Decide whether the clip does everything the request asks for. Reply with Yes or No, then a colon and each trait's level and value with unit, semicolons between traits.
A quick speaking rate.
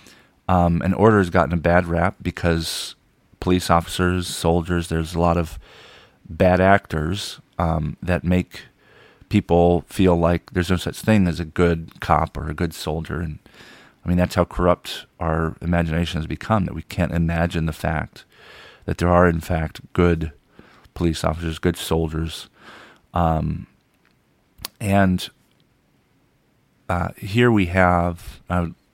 No: average, 145 wpm